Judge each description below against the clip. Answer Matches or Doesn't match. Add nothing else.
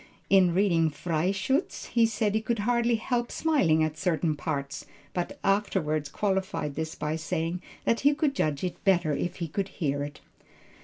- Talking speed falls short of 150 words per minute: Doesn't match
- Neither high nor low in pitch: Matches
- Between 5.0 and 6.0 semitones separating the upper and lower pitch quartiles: Matches